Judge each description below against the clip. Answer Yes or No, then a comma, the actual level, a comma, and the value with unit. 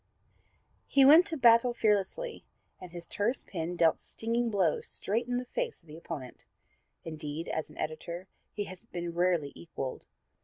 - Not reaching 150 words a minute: No, average, 160 wpm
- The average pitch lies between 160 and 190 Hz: Yes, medium, 185 Hz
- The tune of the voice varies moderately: No, wide, 6.3 semitones